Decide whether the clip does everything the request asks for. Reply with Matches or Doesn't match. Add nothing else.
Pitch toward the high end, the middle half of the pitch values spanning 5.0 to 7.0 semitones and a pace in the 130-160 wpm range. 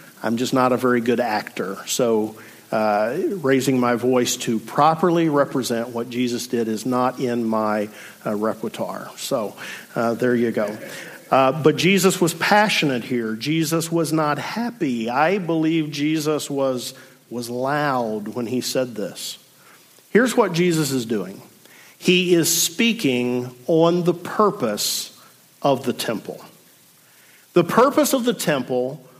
Doesn't match